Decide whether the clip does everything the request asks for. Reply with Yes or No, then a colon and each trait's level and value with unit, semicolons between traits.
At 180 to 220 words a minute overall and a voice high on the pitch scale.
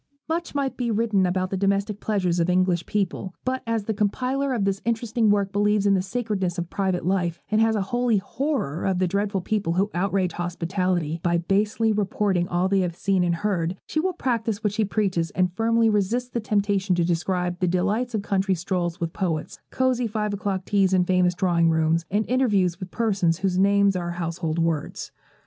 Yes: average, 200 wpm; high, 195 Hz